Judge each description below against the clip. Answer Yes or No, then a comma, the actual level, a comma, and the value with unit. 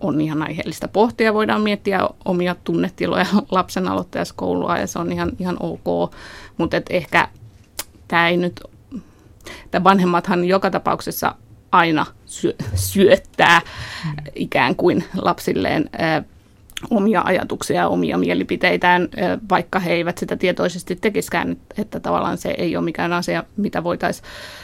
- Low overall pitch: No, medium, 170 Hz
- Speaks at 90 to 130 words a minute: Yes, average, 125 wpm